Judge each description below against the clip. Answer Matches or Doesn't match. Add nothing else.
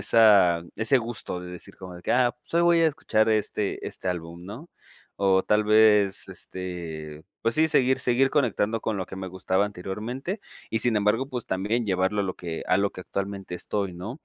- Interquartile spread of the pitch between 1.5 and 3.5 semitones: Doesn't match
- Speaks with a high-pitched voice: Doesn't match